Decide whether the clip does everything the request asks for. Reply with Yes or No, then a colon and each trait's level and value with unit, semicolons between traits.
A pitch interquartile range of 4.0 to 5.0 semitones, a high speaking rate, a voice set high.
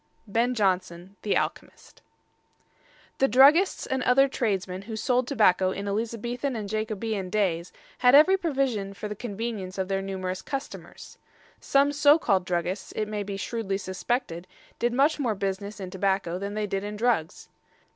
No: average, 4.4 semitones; average, 155 wpm; high, 210 Hz